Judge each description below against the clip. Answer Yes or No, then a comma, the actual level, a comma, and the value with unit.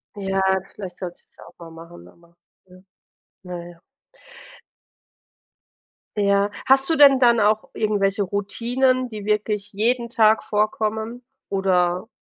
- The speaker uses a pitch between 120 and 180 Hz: No, high, 210 Hz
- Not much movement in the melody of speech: No, average, 3.4 semitones